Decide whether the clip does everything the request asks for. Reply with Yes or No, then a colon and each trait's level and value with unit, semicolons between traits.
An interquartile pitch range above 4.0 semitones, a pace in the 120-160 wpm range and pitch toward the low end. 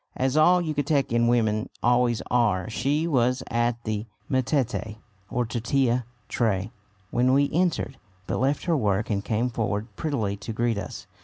No: average, 3.7 semitones; average, 150 wpm; low, 120 Hz